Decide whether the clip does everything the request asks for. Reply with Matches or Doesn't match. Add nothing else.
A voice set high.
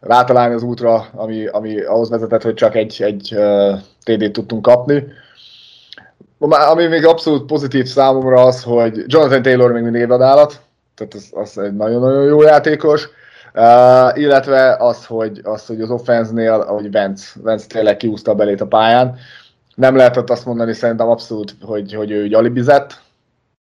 Doesn't match